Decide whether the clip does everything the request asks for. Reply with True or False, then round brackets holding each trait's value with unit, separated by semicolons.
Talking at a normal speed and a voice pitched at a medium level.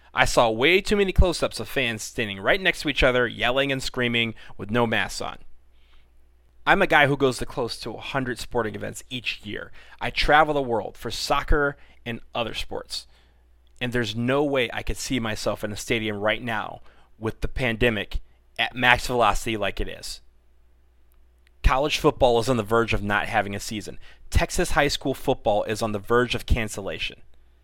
False (190 wpm; 110 Hz)